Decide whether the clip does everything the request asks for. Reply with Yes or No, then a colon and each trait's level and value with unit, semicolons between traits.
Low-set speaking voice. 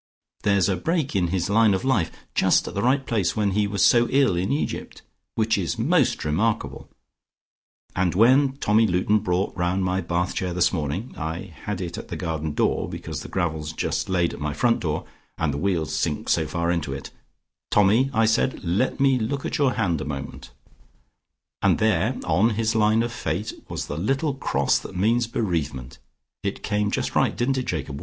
Yes: very low, 95 Hz